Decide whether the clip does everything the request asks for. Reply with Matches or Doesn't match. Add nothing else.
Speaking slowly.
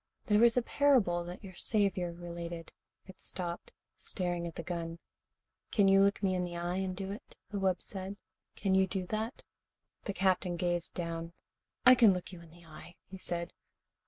Doesn't match